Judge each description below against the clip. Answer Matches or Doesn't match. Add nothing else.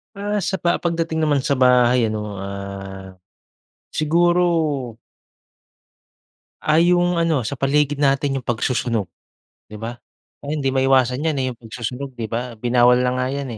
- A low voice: Matches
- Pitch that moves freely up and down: Doesn't match